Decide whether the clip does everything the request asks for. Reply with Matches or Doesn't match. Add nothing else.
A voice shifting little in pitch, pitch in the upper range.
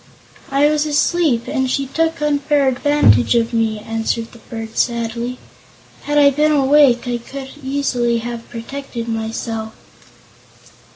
Doesn't match